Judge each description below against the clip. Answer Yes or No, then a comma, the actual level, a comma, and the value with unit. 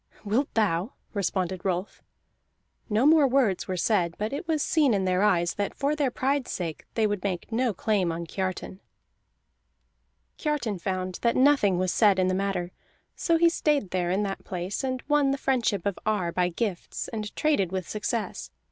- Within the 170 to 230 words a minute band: Yes, average, 180 wpm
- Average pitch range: No, wide, 5.9 semitones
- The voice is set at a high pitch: Yes, high, 205 Hz